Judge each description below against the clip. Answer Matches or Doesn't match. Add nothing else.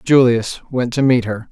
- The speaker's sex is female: Doesn't match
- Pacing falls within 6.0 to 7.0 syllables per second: Doesn't match